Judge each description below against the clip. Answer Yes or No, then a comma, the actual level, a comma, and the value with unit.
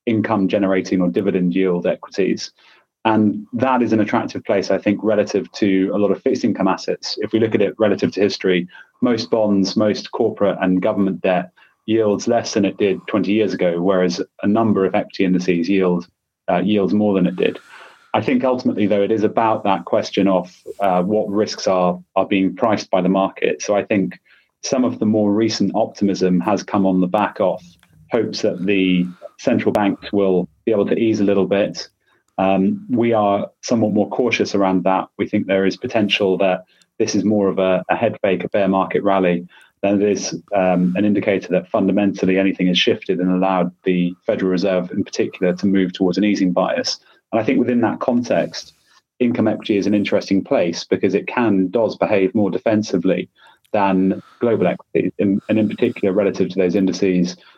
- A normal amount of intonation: No, narrow, 2.0 semitones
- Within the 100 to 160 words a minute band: No, average, 190 wpm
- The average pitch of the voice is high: No, very low, 95 Hz